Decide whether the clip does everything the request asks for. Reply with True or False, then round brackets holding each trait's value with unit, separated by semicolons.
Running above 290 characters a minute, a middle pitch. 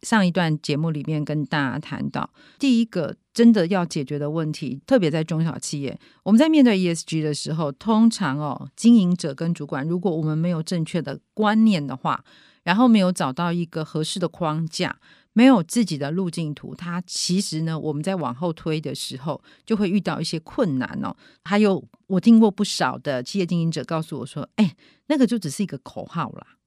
True (310 characters per minute; 170 Hz)